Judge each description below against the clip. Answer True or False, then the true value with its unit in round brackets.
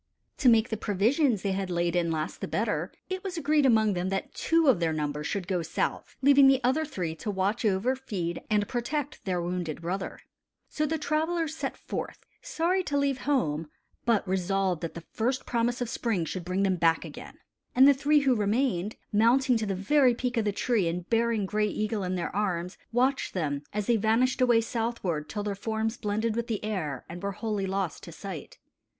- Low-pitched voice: False (215 Hz)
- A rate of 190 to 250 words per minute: True (205 wpm)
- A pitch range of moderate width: False (5.7 semitones)